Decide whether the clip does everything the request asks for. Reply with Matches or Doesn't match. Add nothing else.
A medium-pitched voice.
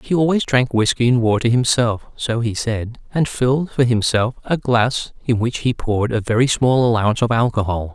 Doesn't match